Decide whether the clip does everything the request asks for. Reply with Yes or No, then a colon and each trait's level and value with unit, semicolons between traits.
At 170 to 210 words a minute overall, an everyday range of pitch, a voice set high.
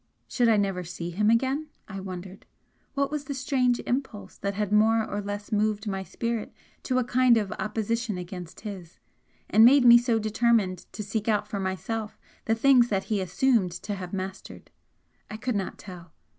Yes: average, 185 wpm; average, 3.5 semitones; high, 210 Hz